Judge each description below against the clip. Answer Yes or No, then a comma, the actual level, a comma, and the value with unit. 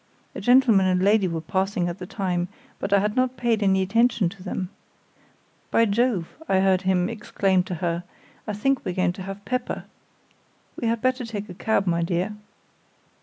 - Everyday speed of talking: Yes, average, 185 wpm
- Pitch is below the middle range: No, high, 195 Hz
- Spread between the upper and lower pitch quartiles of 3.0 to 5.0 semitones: Yes, average, 3.5 semitones